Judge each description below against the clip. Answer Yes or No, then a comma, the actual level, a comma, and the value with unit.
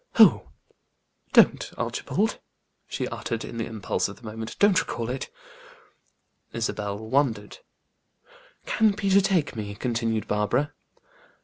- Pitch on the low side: Yes, low, 115 Hz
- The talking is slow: Yes, slow, 115 wpm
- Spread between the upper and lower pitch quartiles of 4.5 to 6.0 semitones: Yes, average, 5.3 semitones